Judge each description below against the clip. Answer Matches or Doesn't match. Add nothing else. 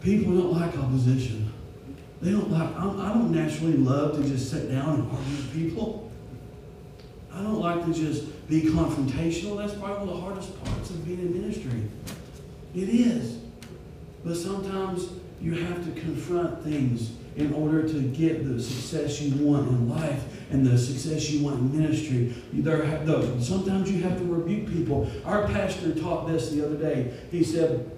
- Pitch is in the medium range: Matches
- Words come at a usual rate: Matches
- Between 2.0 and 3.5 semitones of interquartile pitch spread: Doesn't match